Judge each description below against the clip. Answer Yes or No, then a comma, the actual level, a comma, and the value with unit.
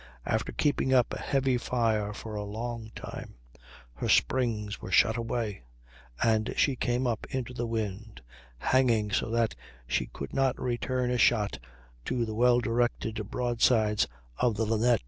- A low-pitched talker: Yes, low, 115 Hz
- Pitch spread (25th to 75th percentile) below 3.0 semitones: Yes, narrow, 2.4 semitones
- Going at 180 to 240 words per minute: No, average, 155 wpm